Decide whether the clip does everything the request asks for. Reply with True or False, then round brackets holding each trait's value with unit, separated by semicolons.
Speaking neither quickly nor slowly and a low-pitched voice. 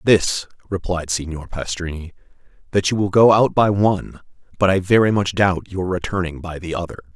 True (175 wpm; 90 Hz)